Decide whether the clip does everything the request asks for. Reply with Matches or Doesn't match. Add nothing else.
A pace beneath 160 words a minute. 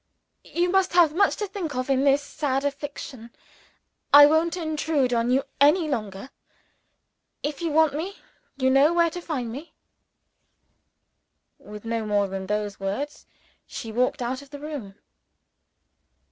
Matches